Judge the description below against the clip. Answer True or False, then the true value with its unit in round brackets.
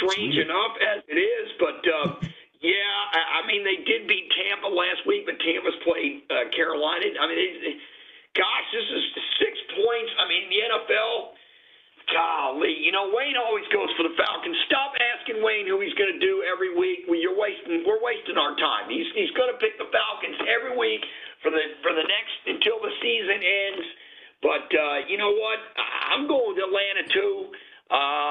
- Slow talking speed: False (190 wpm)